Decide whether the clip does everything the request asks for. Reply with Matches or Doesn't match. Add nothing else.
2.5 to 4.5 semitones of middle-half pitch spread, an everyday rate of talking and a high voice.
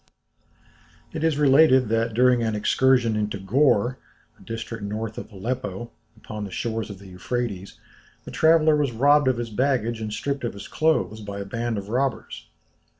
Doesn't match